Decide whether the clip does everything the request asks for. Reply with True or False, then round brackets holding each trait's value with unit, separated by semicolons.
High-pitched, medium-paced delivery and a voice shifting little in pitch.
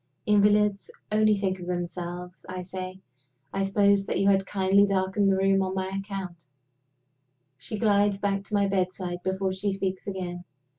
True (195 Hz; 160 wpm; 1.4 semitones)